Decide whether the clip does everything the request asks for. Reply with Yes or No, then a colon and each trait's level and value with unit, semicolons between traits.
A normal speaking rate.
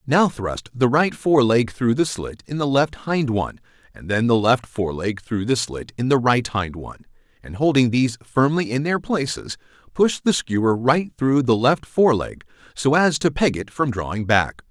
No: fast, 210 wpm